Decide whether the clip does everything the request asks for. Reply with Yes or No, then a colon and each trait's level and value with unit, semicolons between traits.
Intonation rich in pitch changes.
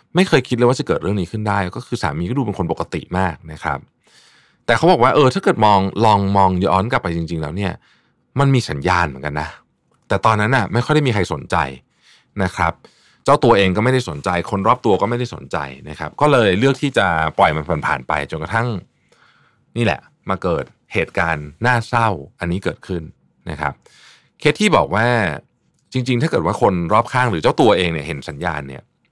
Yes: wide, 6.4 semitones